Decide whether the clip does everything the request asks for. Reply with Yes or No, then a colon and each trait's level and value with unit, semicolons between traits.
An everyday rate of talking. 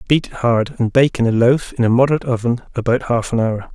No: fast, 240 wpm